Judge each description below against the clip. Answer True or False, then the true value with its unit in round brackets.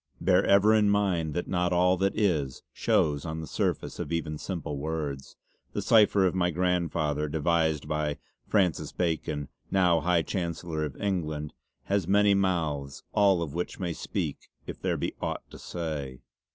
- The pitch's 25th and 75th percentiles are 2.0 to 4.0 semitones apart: True (3.5 semitones)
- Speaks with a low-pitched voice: True (85 Hz)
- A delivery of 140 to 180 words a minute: True (165 wpm)